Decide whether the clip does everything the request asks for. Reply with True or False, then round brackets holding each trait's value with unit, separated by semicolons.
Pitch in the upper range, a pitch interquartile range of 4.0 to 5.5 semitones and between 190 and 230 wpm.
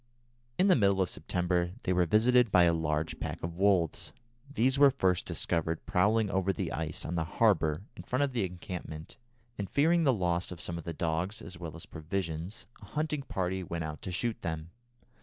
False (90 Hz; 4.7 semitones; 200 wpm)